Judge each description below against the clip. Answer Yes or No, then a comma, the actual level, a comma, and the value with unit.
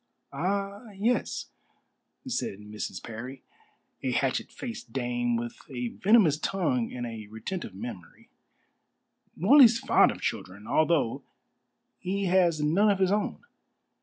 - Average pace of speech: No, slow, 120 wpm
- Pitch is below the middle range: No, medium, 155 Hz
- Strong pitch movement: Yes, wide, 9.0 semitones